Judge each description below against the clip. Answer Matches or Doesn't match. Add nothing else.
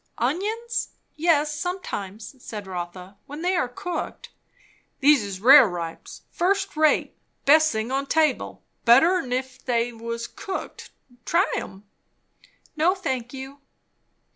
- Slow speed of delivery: Matches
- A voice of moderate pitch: Doesn't match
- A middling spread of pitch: Doesn't match